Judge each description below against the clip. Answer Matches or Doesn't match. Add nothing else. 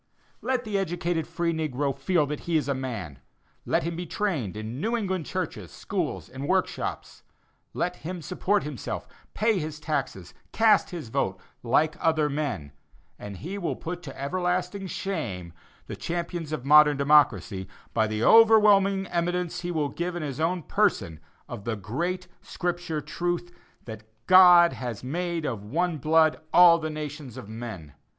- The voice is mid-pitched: Matches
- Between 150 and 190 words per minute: Matches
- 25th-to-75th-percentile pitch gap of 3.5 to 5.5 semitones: Matches